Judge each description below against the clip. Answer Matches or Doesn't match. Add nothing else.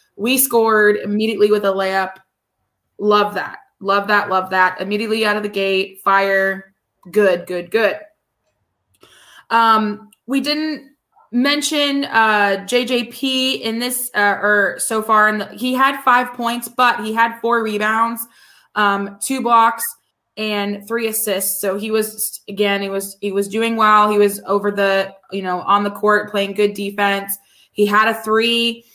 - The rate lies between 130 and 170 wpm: Matches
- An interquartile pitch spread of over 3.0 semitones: Doesn't match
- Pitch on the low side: Doesn't match